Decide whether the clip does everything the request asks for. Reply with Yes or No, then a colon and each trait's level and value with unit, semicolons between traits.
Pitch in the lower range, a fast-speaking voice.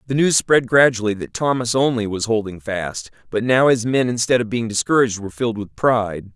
Yes: low, 115 Hz; fast, 210 wpm